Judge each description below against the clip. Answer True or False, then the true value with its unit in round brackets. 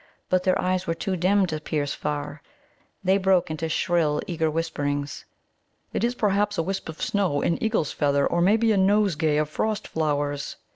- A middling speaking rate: True (180 wpm)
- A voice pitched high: False (170 Hz)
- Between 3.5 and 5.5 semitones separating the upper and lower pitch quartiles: True (4.4 semitones)